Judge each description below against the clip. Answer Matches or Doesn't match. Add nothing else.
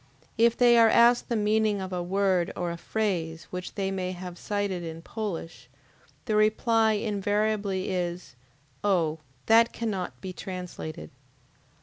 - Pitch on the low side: Doesn't match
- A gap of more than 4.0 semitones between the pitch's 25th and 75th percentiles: Doesn't match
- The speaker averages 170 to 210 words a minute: Doesn't match